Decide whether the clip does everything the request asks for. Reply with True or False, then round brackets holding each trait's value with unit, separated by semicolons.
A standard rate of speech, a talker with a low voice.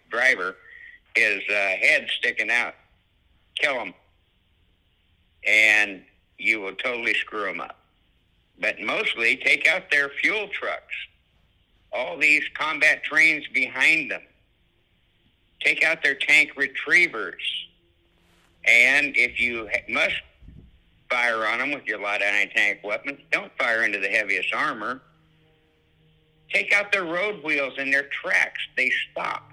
False (130 wpm; 115 Hz)